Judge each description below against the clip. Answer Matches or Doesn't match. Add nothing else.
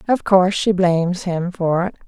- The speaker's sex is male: Doesn't match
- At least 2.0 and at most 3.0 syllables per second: Doesn't match